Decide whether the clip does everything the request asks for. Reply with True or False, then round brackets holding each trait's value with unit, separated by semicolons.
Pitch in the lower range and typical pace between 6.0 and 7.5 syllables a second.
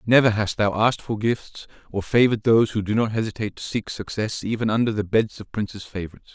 True (110 Hz; 6.4 syllables/s)